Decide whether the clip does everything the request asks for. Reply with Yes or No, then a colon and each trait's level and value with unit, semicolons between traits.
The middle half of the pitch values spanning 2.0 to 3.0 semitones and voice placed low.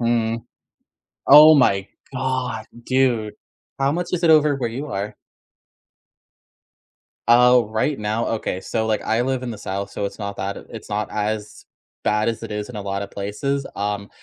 No: average, 3.9 semitones; low, 110 Hz